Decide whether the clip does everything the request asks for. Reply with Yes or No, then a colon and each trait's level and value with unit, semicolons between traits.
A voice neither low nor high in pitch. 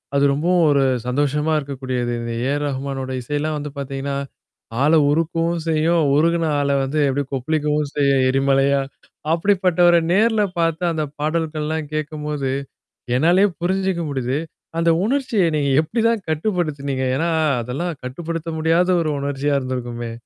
Yes: medium, 150 Hz